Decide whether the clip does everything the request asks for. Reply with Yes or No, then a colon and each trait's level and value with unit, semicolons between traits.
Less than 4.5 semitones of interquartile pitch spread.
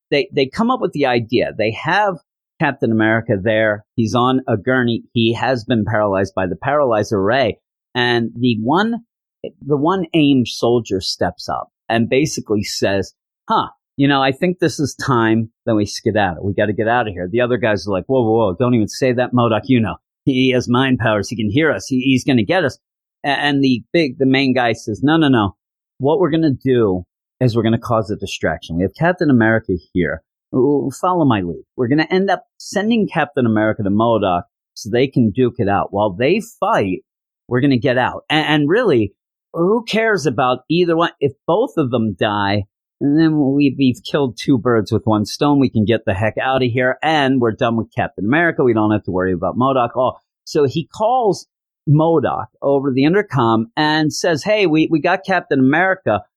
No: average, 4.8 semitones